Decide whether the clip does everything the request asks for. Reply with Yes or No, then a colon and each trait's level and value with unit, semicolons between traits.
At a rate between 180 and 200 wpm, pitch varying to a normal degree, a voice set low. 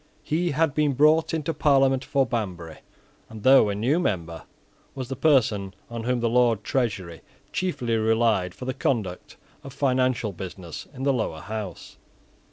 No: average, 160 wpm; average, 5.0 semitones; low, 120 Hz